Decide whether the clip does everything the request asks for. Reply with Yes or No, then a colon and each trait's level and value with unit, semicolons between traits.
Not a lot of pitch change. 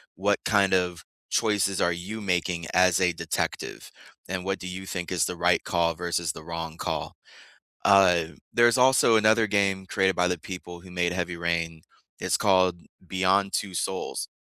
Yes: narrow, 2.1 semitones